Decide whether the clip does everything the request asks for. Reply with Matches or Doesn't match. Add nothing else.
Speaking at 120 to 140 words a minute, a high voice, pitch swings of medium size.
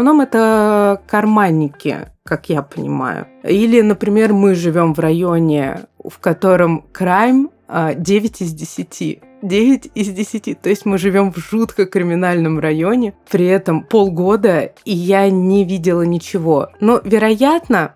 Matches